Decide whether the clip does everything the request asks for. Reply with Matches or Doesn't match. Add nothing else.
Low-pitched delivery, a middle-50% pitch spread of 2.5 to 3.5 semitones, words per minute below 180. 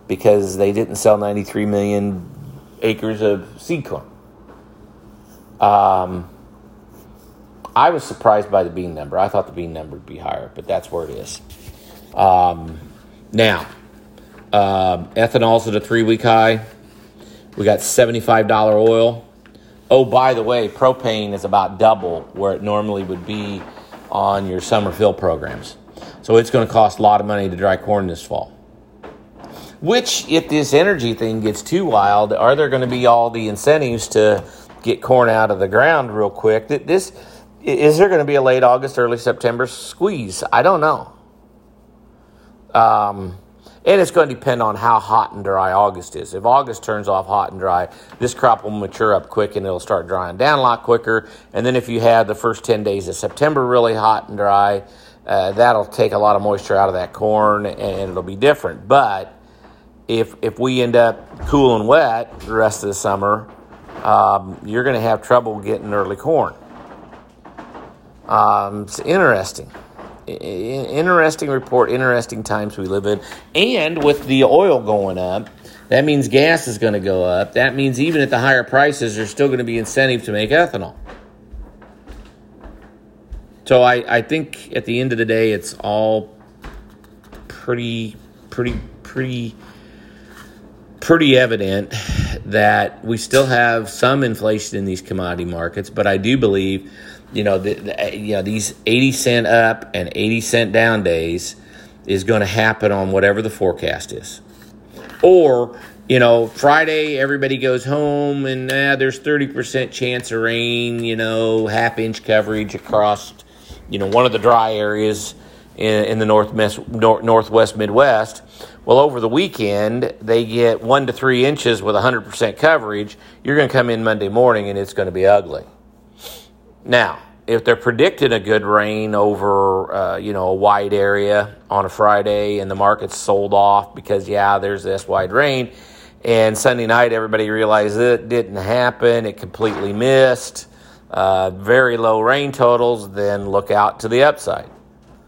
Matches